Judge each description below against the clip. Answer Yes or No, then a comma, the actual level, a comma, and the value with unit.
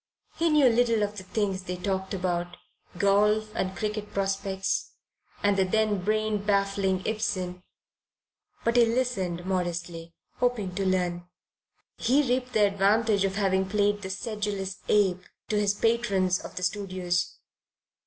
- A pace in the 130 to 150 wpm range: Yes, average, 140 wpm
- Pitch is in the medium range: No, high, 200 Hz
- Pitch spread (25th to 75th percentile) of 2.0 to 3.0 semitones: Yes, narrow, 2.5 semitones